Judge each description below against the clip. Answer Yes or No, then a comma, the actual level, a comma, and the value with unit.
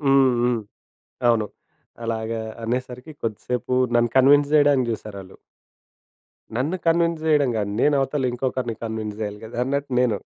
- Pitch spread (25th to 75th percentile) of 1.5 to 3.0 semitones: No, average, 4.0 semitones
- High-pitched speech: No, low, 125 Hz